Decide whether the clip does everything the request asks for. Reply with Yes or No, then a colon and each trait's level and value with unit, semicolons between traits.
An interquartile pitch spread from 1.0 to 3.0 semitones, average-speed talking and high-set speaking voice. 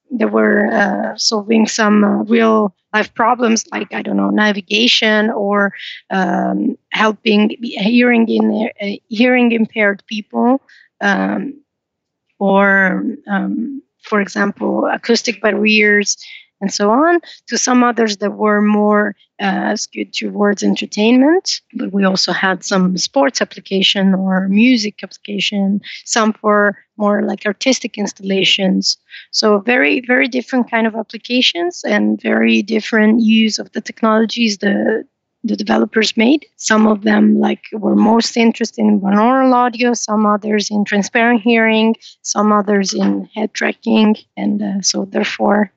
No: narrow, 2.5 semitones; slow, 125 wpm; high, 215 Hz